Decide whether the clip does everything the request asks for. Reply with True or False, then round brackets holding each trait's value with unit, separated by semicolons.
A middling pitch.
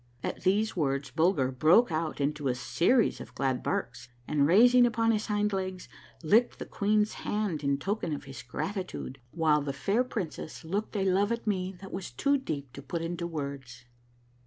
True (175 Hz)